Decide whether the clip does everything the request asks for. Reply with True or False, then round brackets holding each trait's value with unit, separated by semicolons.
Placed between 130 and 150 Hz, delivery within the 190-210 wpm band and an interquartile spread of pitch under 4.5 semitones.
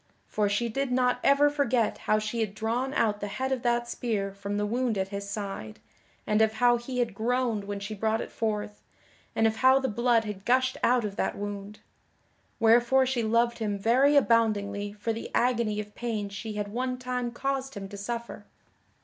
False (225 Hz; 200 wpm; 3.1 semitones)